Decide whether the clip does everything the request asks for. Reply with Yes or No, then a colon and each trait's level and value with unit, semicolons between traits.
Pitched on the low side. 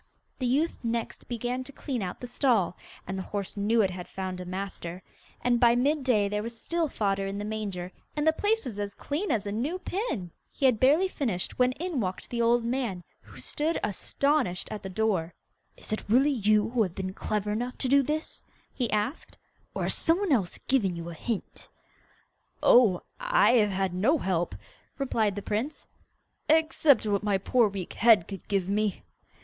No: high, 220 Hz